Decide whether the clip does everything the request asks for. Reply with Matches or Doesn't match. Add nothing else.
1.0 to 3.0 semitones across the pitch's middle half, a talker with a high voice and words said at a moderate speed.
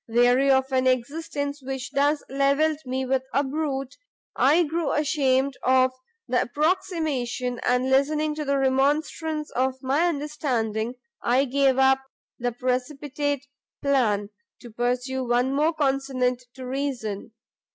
Doesn't match